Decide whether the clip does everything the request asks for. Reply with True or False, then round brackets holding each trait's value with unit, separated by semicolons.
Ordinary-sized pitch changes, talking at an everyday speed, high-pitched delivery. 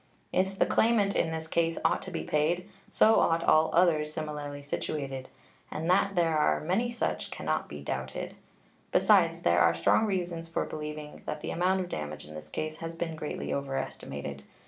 False (3.7 semitones; 185 wpm; 155 Hz)